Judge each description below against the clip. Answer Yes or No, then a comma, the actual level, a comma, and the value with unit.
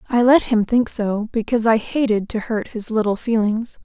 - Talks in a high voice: Yes, high, 225 Hz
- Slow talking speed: No, fast, 205 wpm